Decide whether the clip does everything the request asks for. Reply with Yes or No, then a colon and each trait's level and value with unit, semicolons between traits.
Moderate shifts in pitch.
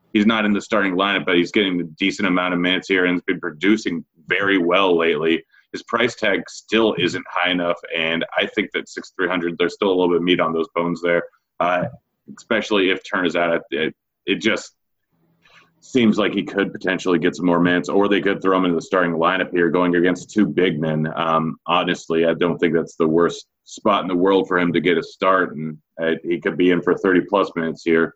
No: narrow, 1.6 semitones